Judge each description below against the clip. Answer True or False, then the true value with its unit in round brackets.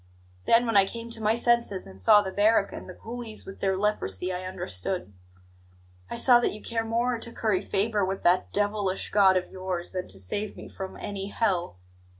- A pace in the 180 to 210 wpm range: True (200 wpm)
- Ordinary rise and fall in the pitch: True (3.4 semitones)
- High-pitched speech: True (200 Hz)